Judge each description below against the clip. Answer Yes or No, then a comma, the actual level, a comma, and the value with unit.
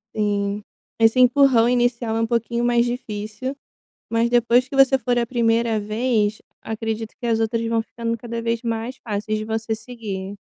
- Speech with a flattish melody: Yes, narrow, 1.7 semitones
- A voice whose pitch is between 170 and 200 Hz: No, high, 230 Hz